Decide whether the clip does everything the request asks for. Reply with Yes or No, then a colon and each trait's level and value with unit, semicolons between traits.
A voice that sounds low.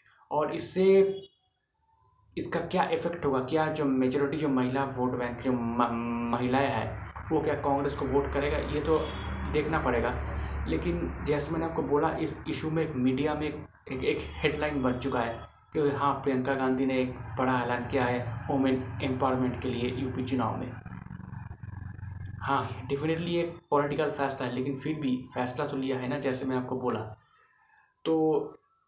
Yes: low, 130 Hz